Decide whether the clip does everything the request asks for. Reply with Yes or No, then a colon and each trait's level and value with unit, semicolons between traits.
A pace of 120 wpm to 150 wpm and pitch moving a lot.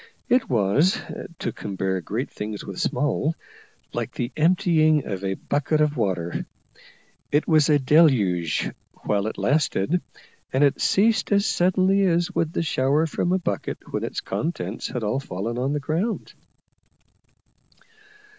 Yes: average, 145 wpm; wide, 8.0 semitones